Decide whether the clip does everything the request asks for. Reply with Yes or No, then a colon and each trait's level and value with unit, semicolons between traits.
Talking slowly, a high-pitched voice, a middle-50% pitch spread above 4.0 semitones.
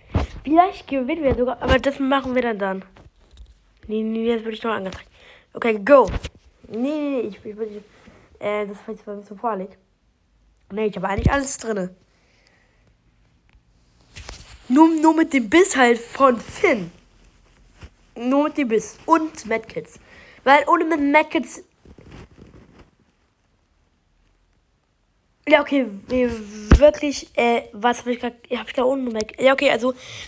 No: average, 140 wpm; high, 245 Hz; average, 4.7 semitones